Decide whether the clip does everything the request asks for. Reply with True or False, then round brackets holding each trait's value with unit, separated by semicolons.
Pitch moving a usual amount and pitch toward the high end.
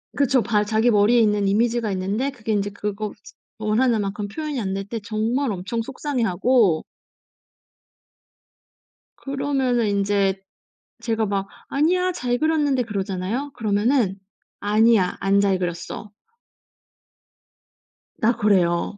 True (3.7 semitones; 215 Hz)